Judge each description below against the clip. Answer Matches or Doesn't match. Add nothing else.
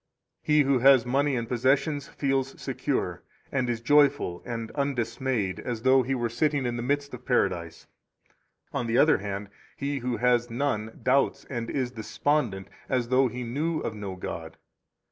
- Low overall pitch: Matches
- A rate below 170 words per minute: Doesn't match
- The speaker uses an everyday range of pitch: Matches